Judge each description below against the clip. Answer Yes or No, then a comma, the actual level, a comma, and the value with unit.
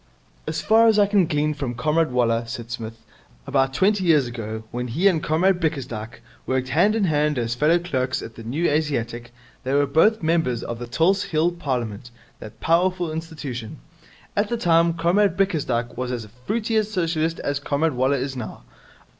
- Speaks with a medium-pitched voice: Yes, medium, 150 Hz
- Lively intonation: Yes, wide, 6.0 semitones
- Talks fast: No, average, 180 wpm